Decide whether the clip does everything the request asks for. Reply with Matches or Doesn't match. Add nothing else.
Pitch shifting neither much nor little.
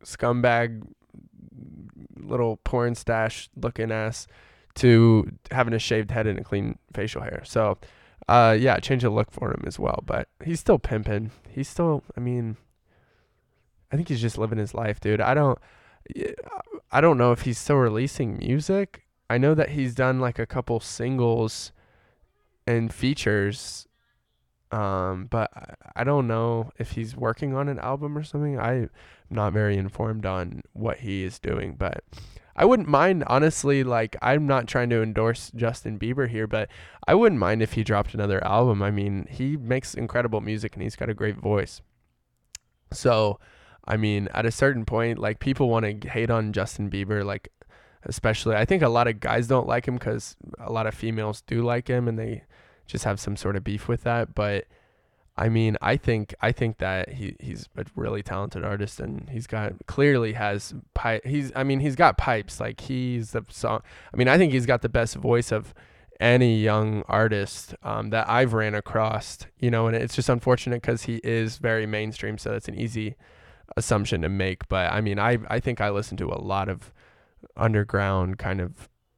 Matches